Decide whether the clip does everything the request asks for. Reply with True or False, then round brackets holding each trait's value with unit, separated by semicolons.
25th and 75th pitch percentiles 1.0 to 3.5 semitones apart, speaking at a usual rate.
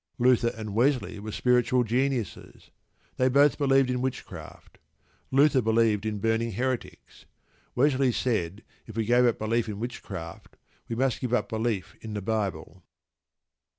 True (2.8 semitones; 145 wpm)